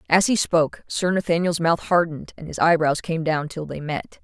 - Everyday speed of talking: No, fast, 215 wpm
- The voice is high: No, medium, 165 Hz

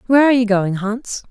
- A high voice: Yes, high, 225 Hz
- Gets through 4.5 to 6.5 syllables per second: Yes, 6.4 syllables/s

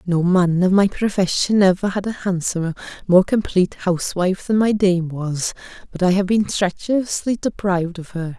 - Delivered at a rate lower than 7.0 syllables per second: Yes, 4.9 syllables/s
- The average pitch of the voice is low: No, medium, 185 Hz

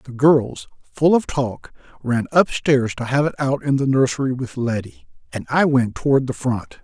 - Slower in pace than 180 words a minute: No, average, 200 wpm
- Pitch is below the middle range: Yes, low, 130 Hz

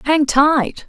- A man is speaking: No, female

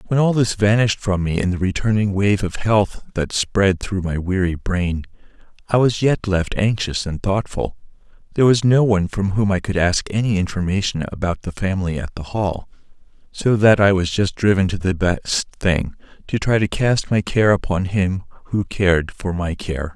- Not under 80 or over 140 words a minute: No, average, 190 wpm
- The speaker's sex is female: No, male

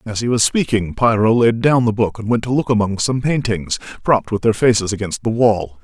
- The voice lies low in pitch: Yes, low, 110 Hz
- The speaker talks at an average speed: No, fast, 235 wpm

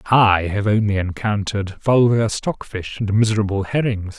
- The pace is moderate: No, slow, 130 wpm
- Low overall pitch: Yes, low, 105 Hz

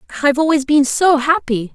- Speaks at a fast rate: No, average, 170 wpm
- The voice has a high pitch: Yes, very high, 280 Hz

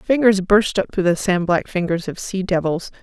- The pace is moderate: No, fast, 220 wpm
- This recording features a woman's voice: Yes, female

